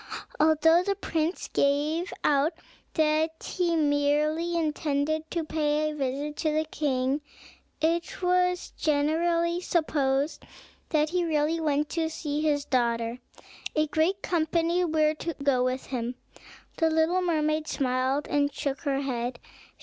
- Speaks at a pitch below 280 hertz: No, very high, 310 Hz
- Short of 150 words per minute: Yes, slow, 135 wpm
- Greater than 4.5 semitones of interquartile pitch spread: No, narrow, 2.4 semitones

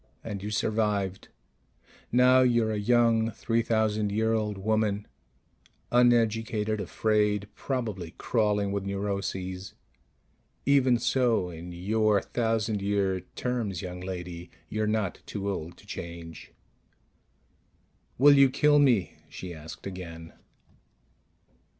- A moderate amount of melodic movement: Yes, average, 3.1 semitones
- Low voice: Yes, low, 105 Hz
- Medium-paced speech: No, slow, 110 wpm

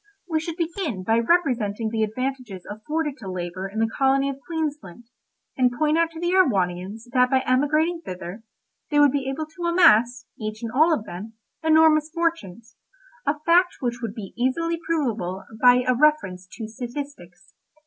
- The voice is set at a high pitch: Yes, very high, 255 Hz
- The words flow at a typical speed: Yes, average, 165 wpm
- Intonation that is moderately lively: No, wide, 6.5 semitones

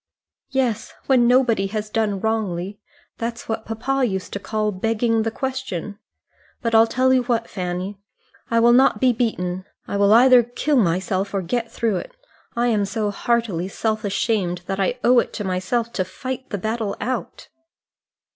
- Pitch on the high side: Yes, high, 225 Hz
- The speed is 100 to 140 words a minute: No, average, 170 wpm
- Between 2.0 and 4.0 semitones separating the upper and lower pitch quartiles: Yes, average, 3.4 semitones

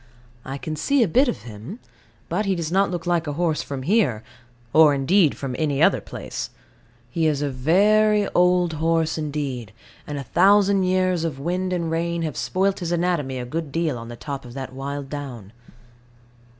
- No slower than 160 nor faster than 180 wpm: No, average, 190 wpm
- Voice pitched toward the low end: No, medium, 160 Hz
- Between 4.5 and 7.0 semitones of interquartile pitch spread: Yes, average, 4.8 semitones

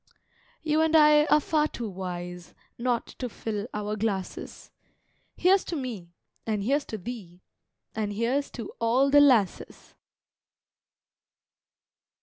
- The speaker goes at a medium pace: No, slow, 125 wpm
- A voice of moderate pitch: No, high, 230 Hz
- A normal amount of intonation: No, wide, 5.9 semitones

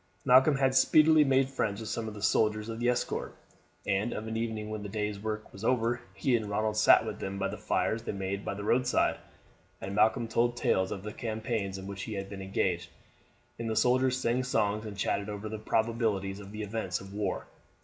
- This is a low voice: Yes, low, 110 Hz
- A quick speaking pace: Yes, fast, 220 wpm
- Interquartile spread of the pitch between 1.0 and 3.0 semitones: Yes, average, 2.7 semitones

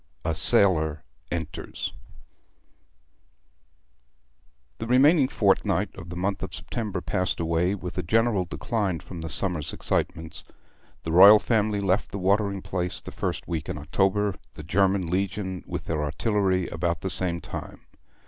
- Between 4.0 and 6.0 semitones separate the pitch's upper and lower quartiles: No, average, 3.4 semitones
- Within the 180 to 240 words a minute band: No, average, 145 wpm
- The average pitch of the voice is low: Yes, very low, 95 Hz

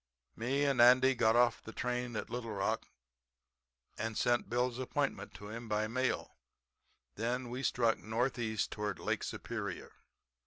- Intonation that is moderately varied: No, narrow, 2.1 semitones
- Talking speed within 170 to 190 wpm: No, average, 145 wpm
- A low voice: Yes, low, 120 Hz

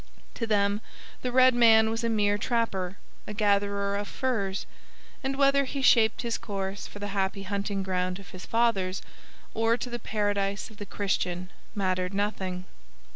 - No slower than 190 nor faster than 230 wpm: No, average, 165 wpm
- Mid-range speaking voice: No, high, 205 Hz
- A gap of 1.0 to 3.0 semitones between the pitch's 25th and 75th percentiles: Yes, average, 2.7 semitones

